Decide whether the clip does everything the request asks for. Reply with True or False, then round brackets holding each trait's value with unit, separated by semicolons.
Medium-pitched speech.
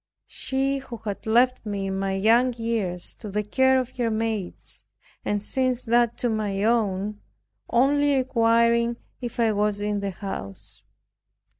False (225 Hz)